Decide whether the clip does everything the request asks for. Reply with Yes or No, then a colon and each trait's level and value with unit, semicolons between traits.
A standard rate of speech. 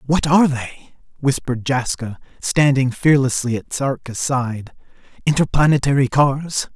No: slow, 105 wpm